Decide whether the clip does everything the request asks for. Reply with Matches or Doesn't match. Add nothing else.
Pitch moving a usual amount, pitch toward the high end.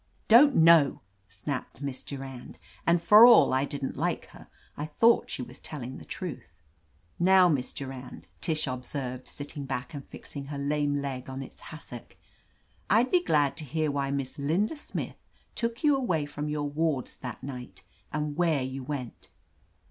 Doesn't match